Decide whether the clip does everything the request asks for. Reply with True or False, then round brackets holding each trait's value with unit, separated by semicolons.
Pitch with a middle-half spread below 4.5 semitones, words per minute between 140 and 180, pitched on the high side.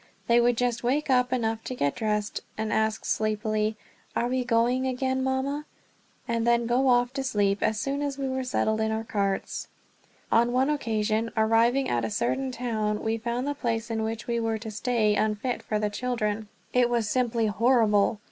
False (2.6 semitones; 190 wpm; 230 Hz)